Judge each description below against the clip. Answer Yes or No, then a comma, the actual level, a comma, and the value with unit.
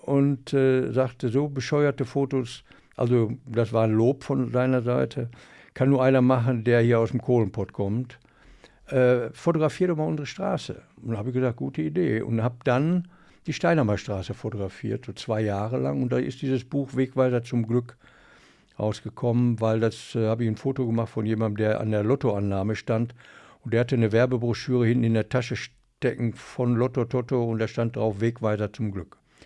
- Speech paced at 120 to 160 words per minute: No, average, 185 wpm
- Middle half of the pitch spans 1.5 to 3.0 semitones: Yes, narrow, 2.6 semitones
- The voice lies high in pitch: No, low, 120 Hz